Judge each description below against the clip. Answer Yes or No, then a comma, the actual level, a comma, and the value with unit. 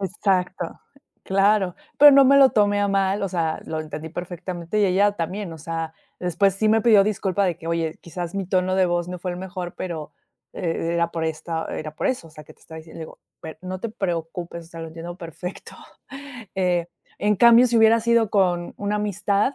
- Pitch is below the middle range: No, medium, 180 Hz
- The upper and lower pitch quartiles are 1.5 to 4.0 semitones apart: Yes, average, 3.4 semitones